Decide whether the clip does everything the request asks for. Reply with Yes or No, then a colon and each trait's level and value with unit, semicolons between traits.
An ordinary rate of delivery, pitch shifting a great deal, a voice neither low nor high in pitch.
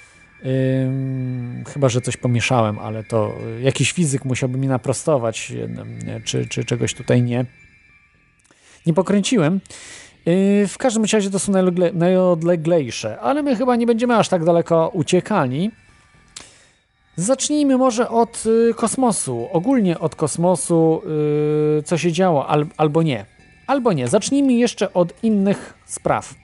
Yes: average, 130 wpm; wide, 7.6 semitones; medium, 170 Hz